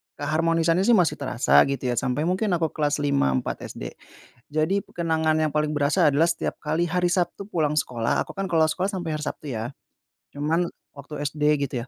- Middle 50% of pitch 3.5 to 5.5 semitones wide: No, average, 2.9 semitones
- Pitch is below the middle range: No, medium, 155 Hz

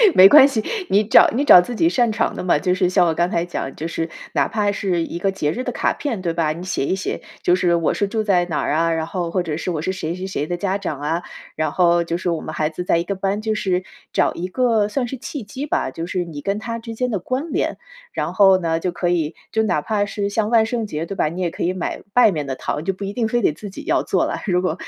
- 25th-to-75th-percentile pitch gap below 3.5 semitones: No, average, 4.0 semitones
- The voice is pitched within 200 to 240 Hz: No, medium, 185 Hz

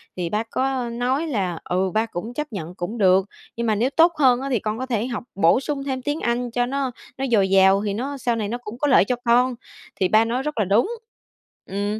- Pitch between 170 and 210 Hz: No, high, 235 Hz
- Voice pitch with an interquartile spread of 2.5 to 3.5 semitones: No, average, 4.3 semitones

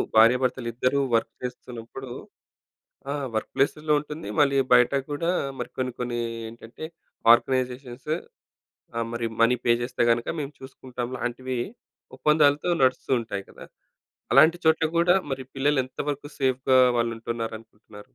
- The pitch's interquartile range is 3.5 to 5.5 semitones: No, average, 3.1 semitones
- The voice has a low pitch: Yes, low, 130 Hz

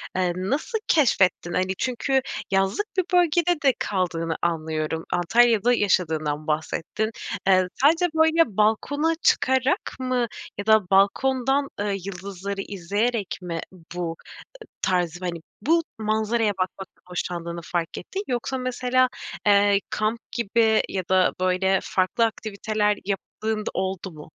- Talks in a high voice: Yes, high, 205 Hz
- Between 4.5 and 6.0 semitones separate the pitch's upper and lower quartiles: Yes, average, 5.2 semitones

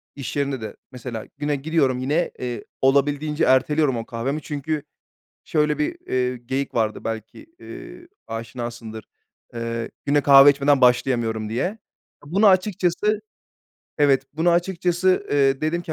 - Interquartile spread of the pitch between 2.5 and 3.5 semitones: No, average, 4.1 semitones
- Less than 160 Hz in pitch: Yes, medium, 140 Hz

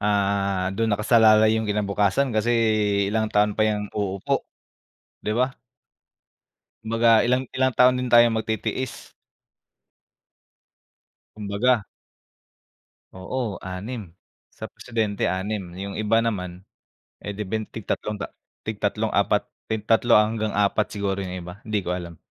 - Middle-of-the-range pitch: No, low, 105 Hz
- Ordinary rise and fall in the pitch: No, narrow, 2.3 semitones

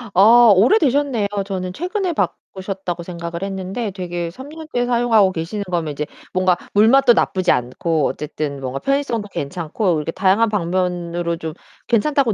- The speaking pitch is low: No, high, 190 Hz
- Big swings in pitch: Yes, wide, 5.7 semitones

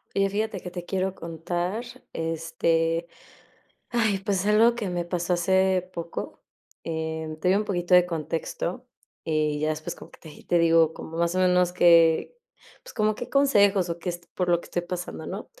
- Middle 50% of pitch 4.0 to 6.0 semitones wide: No, narrow, 2.6 semitones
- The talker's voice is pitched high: No, medium, 175 Hz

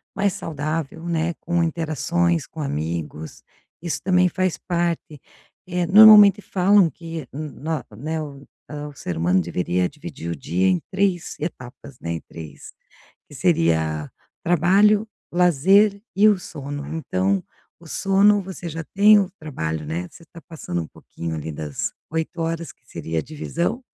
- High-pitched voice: No, medium, 160 Hz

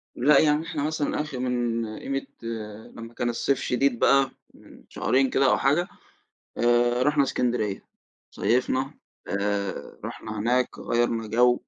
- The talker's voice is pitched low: Yes, low, 125 Hz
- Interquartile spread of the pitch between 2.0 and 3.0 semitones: Yes, average, 2.7 semitones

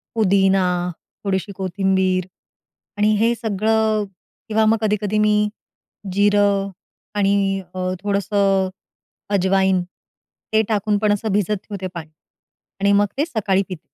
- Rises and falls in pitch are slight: Yes, narrow, 1.7 semitones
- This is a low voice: No, high, 200 Hz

